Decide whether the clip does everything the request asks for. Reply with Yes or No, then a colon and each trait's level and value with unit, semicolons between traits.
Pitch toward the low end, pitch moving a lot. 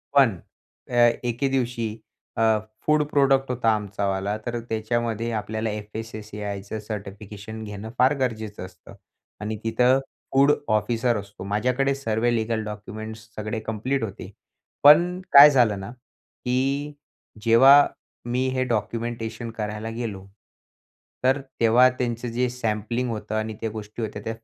No: low, 115 Hz; average, 2.9 semitones